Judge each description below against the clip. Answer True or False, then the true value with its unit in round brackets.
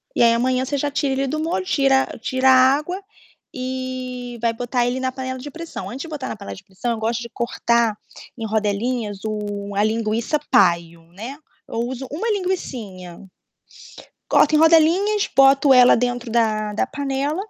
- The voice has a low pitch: False (255 Hz)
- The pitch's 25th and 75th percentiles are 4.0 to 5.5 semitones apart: False (3.6 semitones)